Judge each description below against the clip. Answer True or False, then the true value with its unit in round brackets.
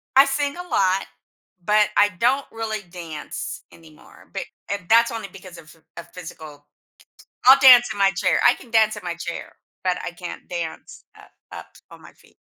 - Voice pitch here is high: True (200 Hz)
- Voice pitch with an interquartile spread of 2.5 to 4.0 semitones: False (5.2 semitones)